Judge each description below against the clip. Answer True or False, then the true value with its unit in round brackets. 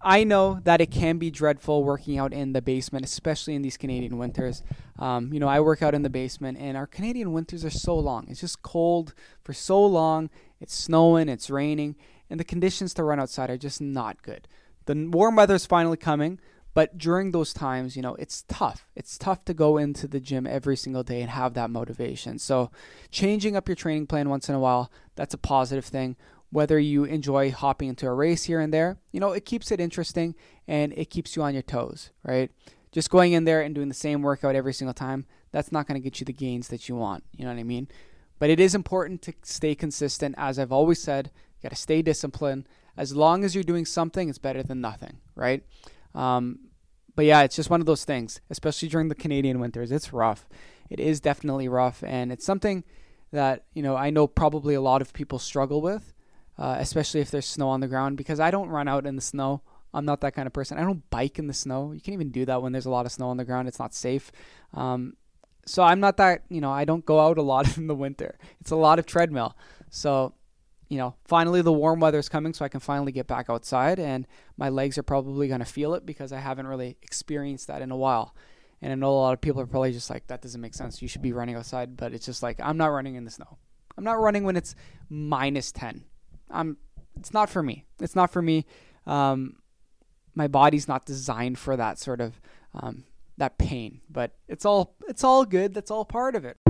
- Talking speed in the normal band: False (235 wpm)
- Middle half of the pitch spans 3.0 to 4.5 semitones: True (3.6 semitones)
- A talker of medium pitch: True (145 Hz)